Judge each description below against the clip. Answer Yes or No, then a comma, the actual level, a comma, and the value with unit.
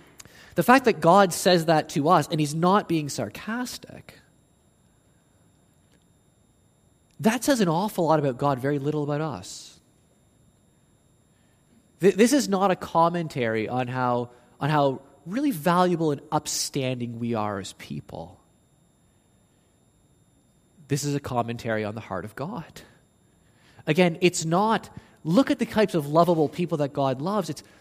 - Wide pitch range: Yes, wide, 6.1 semitones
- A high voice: No, medium, 155 Hz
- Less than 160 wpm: Yes, average, 140 wpm